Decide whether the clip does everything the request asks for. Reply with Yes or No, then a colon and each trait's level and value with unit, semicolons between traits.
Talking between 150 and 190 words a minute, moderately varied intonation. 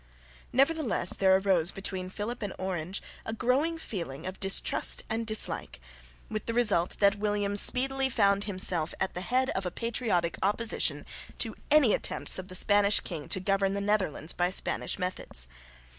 Yes: average, 160 wpm; average, 3.6 semitones